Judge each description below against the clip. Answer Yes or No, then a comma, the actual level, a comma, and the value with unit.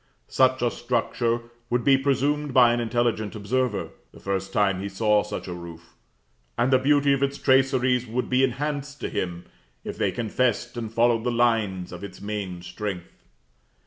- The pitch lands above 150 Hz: No, low, 120 Hz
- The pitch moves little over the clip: No, average, 4.2 semitones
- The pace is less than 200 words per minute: Yes, average, 175 wpm